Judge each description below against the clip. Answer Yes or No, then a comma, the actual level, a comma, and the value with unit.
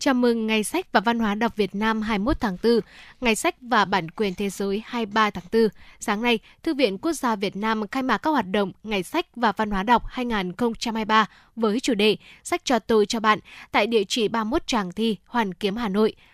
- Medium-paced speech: Yes, average, 225 wpm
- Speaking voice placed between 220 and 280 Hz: Yes, high, 225 Hz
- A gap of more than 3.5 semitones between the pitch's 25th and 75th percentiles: No, narrow, 2.6 semitones